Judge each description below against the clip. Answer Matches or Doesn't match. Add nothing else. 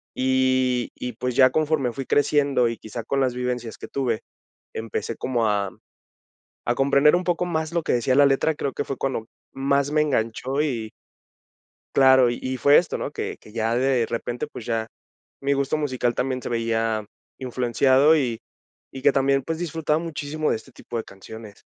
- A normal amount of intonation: Matches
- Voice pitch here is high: Doesn't match